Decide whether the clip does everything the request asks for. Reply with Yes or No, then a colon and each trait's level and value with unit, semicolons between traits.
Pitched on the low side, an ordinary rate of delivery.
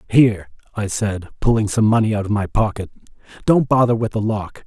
Yes: low, 110 Hz; average, 195 wpm